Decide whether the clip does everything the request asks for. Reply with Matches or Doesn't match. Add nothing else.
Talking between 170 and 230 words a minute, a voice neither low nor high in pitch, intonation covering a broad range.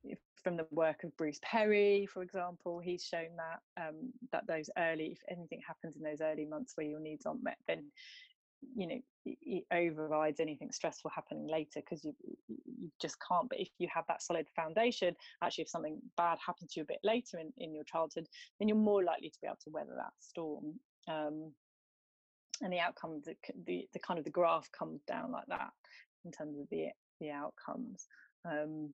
Doesn't match